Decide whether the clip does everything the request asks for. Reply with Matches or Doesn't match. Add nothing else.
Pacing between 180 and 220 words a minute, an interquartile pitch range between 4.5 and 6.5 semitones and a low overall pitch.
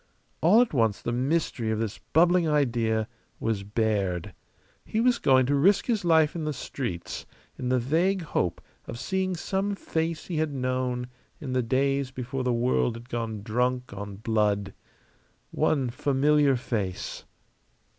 Doesn't match